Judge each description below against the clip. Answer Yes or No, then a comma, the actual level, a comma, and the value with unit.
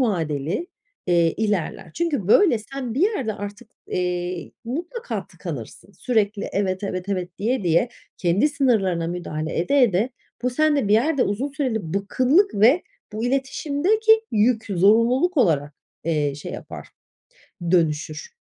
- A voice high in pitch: Yes, high, 215 Hz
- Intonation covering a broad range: Yes, wide, 7.3 semitones